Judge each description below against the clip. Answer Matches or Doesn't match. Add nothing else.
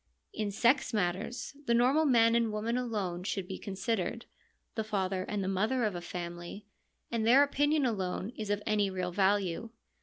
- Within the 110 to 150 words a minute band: Doesn't match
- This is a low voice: Doesn't match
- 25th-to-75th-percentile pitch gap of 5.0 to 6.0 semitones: Doesn't match